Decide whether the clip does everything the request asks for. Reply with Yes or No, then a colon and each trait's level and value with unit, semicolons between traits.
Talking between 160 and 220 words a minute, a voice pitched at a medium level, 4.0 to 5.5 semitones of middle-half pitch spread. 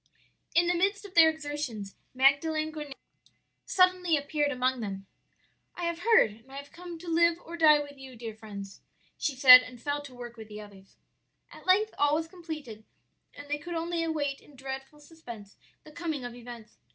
No: average, 185 wpm; very high, 290 Hz; average, 5.1 semitones